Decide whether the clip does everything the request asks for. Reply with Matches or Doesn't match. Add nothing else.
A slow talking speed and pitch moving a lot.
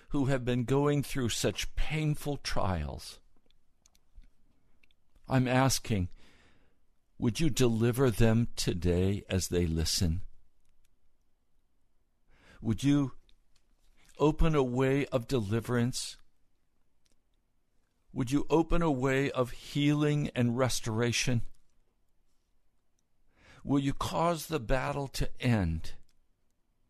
Matches